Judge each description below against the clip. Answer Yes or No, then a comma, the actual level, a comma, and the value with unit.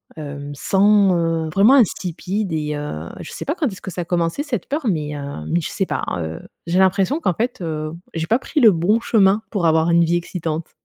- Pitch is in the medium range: Yes, medium, 175 Hz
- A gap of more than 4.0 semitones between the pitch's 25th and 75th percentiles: Yes, average, 4.7 semitones